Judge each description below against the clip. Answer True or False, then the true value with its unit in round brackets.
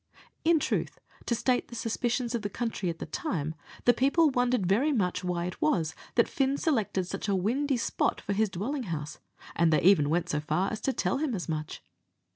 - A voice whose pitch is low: False (215 Hz)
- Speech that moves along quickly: True (210 wpm)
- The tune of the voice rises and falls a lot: True (6.3 semitones)